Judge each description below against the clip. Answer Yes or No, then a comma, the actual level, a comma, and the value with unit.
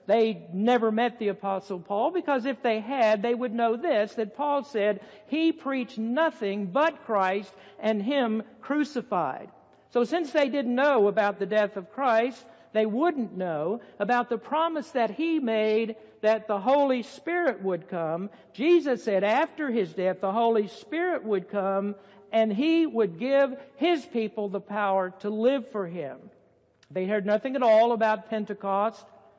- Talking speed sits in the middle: Yes, average, 160 wpm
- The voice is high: Yes, high, 225 Hz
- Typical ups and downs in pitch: Yes, average, 4.8 semitones